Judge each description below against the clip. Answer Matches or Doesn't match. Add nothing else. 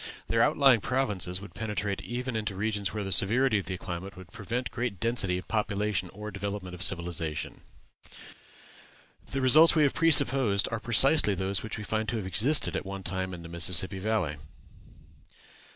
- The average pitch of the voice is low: Matches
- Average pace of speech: Matches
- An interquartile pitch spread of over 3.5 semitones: Matches